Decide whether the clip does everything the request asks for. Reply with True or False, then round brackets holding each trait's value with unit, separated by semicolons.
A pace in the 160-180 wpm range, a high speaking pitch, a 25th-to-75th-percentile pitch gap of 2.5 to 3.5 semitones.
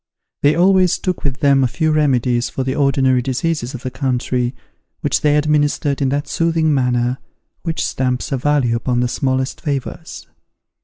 False (165 wpm; 135 Hz; 2.9 semitones)